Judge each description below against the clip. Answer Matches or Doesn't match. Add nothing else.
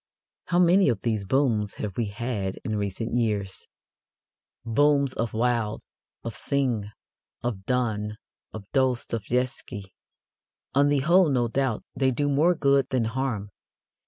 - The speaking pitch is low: Matches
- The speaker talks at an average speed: Doesn't match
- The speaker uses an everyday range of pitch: Matches